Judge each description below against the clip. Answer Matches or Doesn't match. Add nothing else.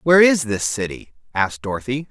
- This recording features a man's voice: Matches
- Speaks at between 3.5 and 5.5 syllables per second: Doesn't match